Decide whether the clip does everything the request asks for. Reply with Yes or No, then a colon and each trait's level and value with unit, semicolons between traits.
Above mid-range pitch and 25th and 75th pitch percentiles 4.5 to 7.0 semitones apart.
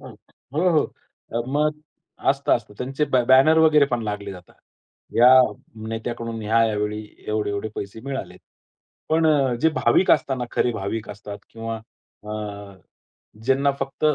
No: low, 115 Hz; average, 4.8 semitones